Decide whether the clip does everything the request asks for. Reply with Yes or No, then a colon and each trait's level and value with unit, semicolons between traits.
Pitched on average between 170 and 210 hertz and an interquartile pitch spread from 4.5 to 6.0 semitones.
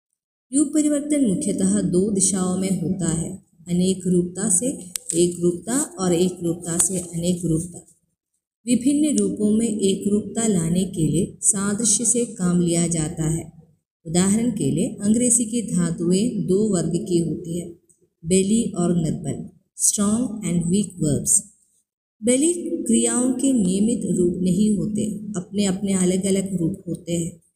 No: high, 190 Hz; average, 3.5 semitones